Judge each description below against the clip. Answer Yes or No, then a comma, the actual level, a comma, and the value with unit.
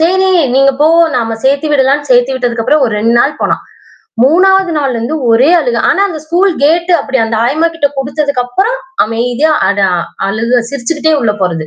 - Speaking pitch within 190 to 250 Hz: No, very high, 275 Hz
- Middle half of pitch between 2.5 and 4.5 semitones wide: No, average, 5.0 semitones